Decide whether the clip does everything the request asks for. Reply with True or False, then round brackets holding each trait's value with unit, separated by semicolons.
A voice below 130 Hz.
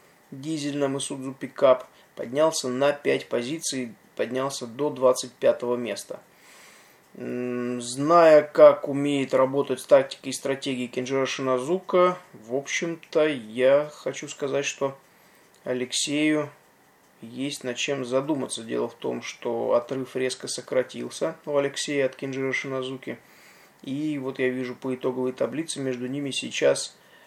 False (135 Hz)